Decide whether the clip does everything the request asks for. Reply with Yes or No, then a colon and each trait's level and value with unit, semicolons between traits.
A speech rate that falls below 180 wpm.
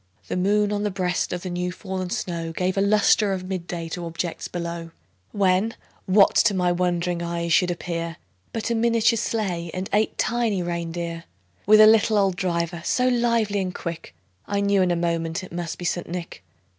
No: average, 195 wpm